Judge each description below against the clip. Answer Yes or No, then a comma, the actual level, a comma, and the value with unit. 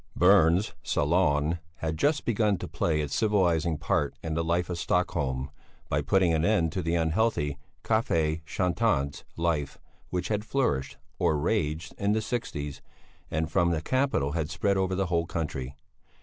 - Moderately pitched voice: No, very low, 85 Hz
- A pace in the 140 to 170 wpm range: Yes, average, 160 wpm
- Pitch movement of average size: Yes, average, 3.9 semitones